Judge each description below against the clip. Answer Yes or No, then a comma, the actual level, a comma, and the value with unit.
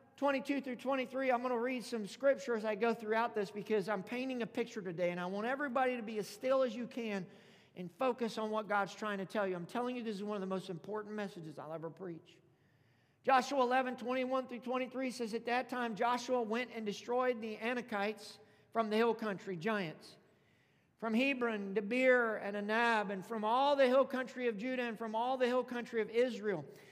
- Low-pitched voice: No, high, 230 Hz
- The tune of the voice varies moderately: Yes, average, 3.5 semitones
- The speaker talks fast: Yes, fast, 210 wpm